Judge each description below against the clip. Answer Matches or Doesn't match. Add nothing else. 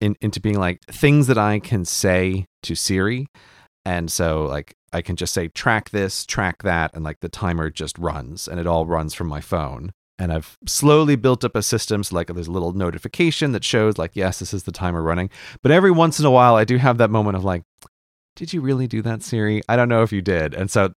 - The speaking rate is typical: Doesn't match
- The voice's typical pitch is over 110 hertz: Doesn't match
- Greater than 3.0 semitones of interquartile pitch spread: Matches